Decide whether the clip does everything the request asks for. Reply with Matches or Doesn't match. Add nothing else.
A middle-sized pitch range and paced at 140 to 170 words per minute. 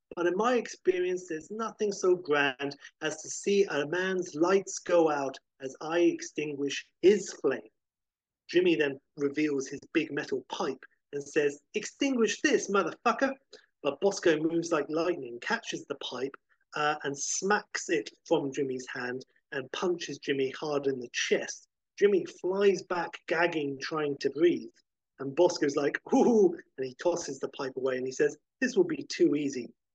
Doesn't match